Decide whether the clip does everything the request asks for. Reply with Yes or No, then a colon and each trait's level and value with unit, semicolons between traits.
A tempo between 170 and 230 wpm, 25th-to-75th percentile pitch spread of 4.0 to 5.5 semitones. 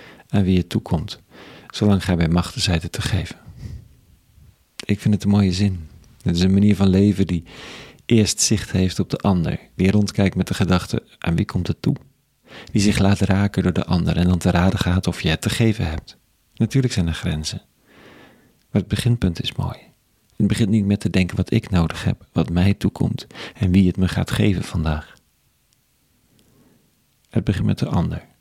No: average, 195 wpm; average, 2.7 semitones